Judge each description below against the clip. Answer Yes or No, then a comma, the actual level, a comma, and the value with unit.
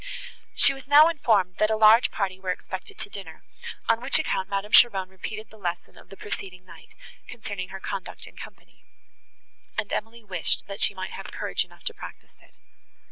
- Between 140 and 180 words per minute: No, average, 190 wpm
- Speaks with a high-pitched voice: Yes, high, 205 Hz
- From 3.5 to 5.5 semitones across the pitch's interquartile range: No, average, 3.1 semitones